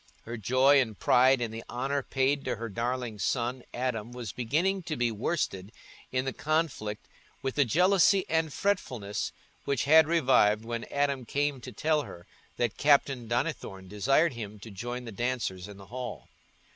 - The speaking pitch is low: Yes, low, 125 Hz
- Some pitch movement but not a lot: Yes, average, 4.0 semitones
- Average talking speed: Yes, average, 170 wpm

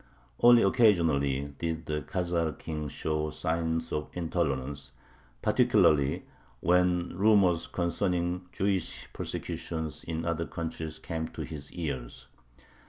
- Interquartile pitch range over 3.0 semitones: No, narrow, 2.6 semitones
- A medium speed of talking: No, slow, 105 wpm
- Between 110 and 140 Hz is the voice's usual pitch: No, very low, 80 Hz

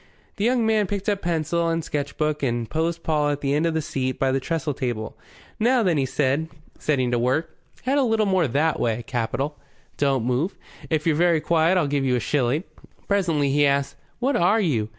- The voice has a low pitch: No, medium, 150 Hz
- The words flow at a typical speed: No, fast, 210 wpm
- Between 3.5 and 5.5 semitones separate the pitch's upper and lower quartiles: Yes, average, 4.1 semitones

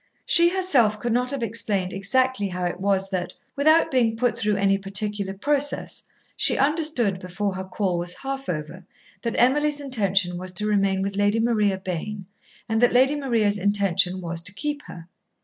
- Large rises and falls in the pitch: No, average, 5.0 semitones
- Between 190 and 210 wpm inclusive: No, average, 175 wpm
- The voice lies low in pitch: No, high, 205 Hz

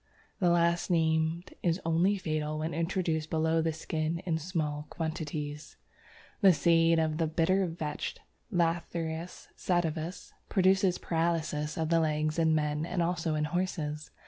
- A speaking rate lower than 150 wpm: Yes, average, 140 wpm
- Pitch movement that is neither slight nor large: No, narrow, 1.8 semitones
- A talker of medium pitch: Yes, medium, 165 Hz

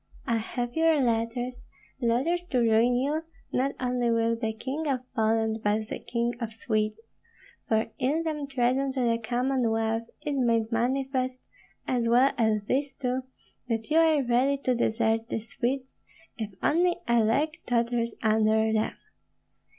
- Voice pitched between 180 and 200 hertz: No, high, 240 Hz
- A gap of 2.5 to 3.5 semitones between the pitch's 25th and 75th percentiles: Yes, average, 2.9 semitones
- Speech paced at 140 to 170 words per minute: Yes, average, 150 wpm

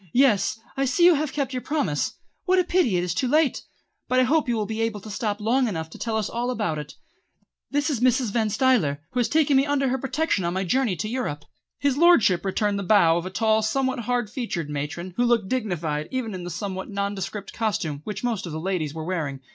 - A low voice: No, high, 220 Hz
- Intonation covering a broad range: Yes, wide, 6.1 semitones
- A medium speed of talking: No, fast, 235 wpm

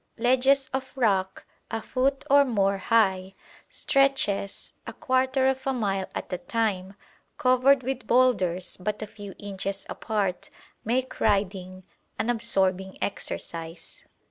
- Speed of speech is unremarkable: No, slow, 125 wpm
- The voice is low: No, high, 215 Hz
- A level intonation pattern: No, average, 5.1 semitones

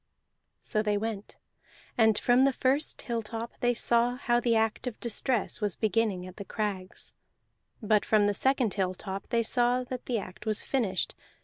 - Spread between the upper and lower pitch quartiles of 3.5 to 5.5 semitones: No, average, 2.9 semitones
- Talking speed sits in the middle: Yes, average, 170 wpm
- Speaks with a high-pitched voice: Yes, high, 225 Hz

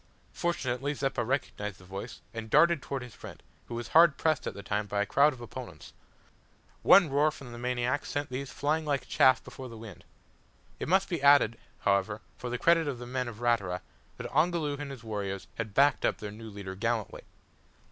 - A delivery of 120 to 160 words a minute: No, average, 200 wpm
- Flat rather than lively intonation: No, average, 4.9 semitones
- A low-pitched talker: Yes, low, 125 Hz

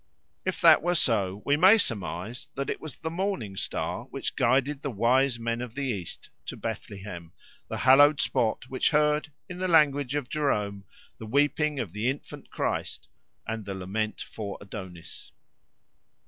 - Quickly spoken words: No, average, 160 wpm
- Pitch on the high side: No, low, 125 Hz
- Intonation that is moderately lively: No, wide, 6.1 semitones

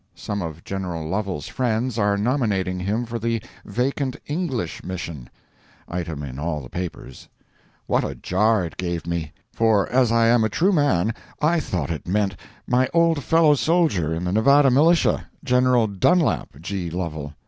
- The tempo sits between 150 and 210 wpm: Yes, average, 160 wpm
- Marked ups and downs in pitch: Yes, wide, 6.7 semitones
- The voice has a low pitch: Yes, low, 105 Hz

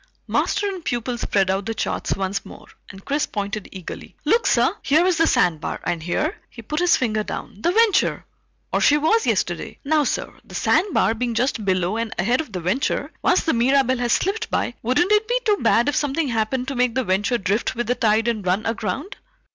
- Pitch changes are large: Yes, wide, 6.6 semitones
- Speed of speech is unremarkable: No, fast, 210 wpm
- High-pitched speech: Yes, high, 240 Hz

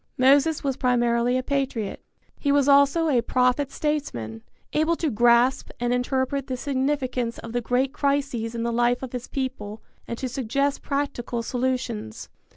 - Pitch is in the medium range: No, very high, 255 Hz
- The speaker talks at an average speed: Yes, average, 160 wpm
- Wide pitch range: No, average, 2.7 semitones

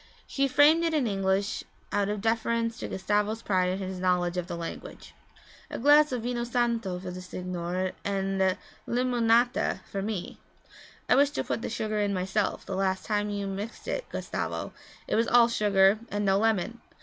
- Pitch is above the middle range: Yes, high, 205 Hz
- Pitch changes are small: No, average, 3.7 semitones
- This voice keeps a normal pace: Yes, average, 180 wpm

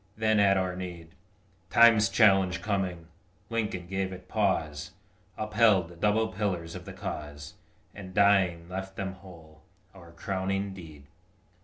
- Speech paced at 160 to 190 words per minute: No, slow, 135 wpm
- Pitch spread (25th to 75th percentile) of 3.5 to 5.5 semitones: No, average, 2.9 semitones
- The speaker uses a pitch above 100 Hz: No, very low, 95 Hz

